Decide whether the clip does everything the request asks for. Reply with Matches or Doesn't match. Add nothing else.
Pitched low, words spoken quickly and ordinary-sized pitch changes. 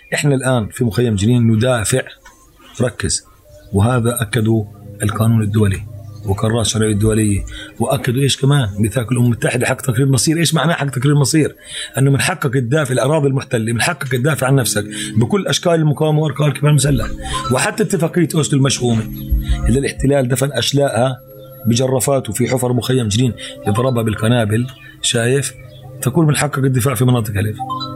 Matches